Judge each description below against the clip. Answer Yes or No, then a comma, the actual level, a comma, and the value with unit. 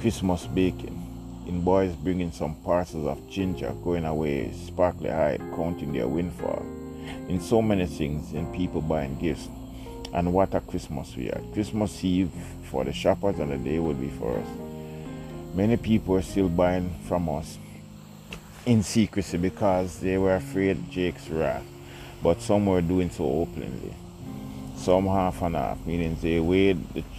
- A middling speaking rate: Yes, average, 160 wpm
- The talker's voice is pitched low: Yes, very low, 85 Hz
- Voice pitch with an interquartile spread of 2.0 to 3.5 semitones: Yes, average, 3.2 semitones